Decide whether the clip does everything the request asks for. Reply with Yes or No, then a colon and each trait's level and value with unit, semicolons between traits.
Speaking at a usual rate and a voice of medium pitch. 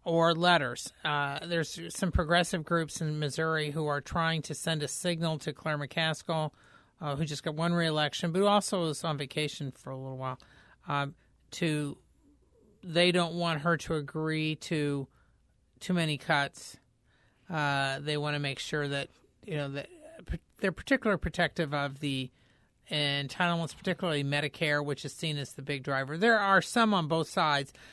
Yes: average, 165 wpm; medium, 155 Hz